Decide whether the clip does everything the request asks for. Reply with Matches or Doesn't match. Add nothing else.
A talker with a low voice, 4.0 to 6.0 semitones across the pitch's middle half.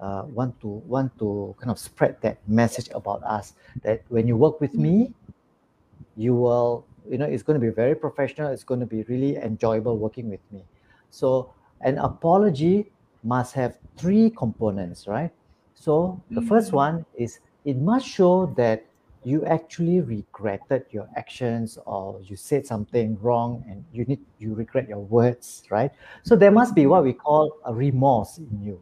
Matches